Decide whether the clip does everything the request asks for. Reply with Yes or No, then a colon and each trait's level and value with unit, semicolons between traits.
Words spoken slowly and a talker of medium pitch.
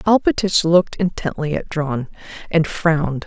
Yes: slow, 130 wpm; medium, 165 Hz